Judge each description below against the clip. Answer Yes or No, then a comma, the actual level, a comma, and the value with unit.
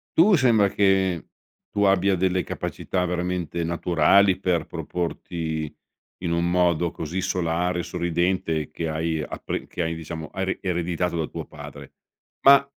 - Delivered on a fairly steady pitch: Yes, narrow, 2.2 semitones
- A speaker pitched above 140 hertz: No, very low, 90 Hz